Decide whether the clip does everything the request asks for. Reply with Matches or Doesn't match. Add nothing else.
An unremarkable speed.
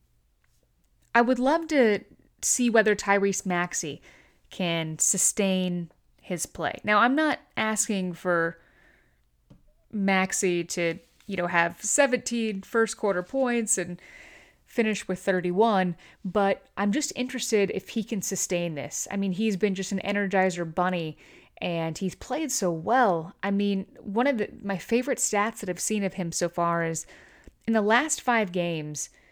Matches